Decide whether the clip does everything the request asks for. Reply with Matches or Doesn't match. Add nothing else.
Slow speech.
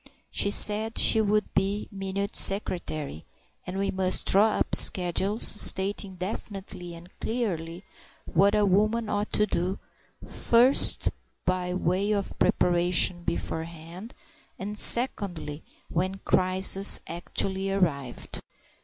Matches